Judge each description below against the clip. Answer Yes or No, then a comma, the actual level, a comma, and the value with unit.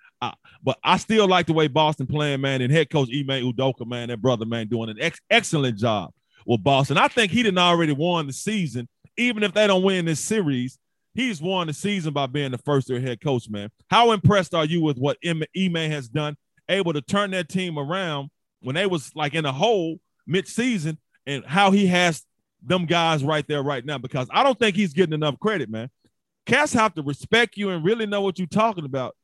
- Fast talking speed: Yes, fast, 220 wpm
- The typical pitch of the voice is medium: Yes, medium, 160 Hz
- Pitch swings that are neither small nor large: No, wide, 5.7 semitones